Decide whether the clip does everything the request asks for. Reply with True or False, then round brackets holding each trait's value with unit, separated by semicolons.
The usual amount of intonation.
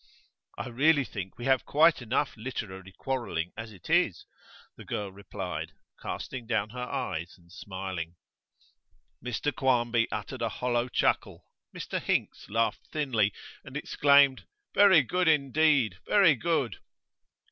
False (5.7 semitones)